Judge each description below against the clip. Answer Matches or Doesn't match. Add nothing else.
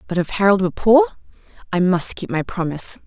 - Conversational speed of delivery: Matches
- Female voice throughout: Matches